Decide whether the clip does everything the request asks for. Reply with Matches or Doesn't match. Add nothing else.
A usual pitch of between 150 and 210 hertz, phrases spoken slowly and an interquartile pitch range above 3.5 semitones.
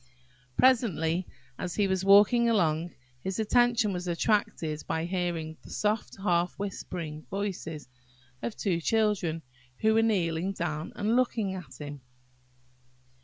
Matches